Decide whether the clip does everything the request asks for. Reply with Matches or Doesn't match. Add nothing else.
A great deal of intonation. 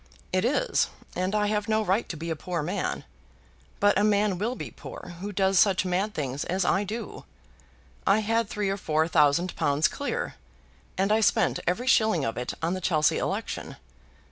Doesn't match